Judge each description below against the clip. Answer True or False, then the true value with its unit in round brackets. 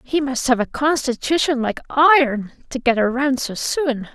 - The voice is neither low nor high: False (265 Hz)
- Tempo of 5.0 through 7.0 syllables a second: False (4.6 syllables/s)